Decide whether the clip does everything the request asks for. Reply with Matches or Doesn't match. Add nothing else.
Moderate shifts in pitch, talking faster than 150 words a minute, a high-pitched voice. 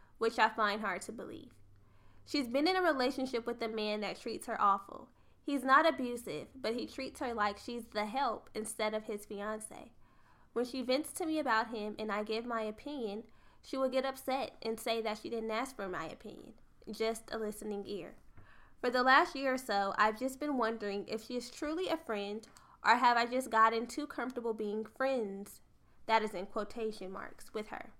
Matches